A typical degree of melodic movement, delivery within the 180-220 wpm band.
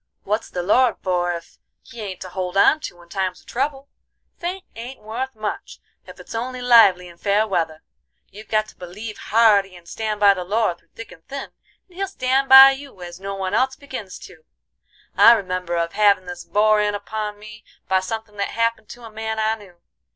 Yes: average, 3.8 semitones; fast, 205 wpm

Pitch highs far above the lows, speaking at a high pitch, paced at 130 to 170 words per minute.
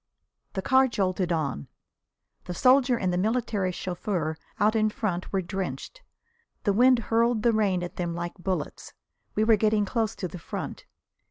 No: average, 4.1 semitones; high, 200 Hz; average, 165 wpm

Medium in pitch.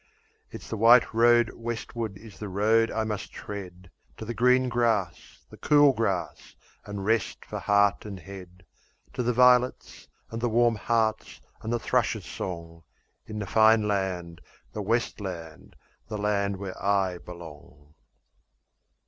No: low, 105 Hz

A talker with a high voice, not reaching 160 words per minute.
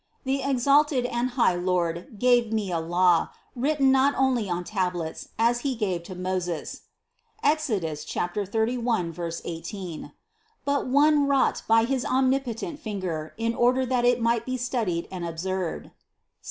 Yes: high, 225 Hz; average, 150 wpm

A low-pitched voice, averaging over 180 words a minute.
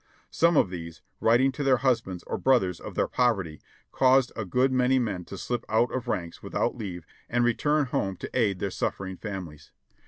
Yes: low, 115 Hz; average, 195 wpm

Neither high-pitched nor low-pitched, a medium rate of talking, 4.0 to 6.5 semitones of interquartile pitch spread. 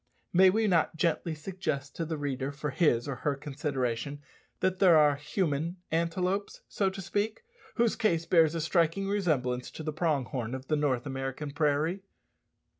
Yes: medium, 155 Hz; average, 170 wpm; average, 4.4 semitones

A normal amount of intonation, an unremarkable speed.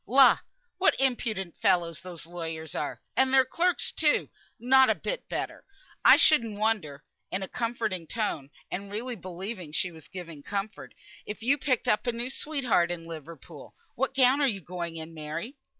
No: wide, 7.0 semitones; average, 170 wpm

